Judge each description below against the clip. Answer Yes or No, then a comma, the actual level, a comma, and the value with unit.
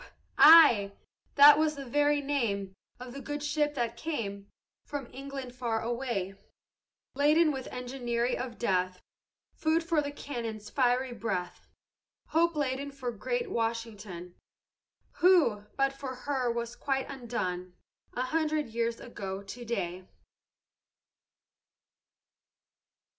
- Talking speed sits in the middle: No, slow, 115 wpm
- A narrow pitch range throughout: No, average, 4.3 semitones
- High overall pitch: Yes, very high, 250 Hz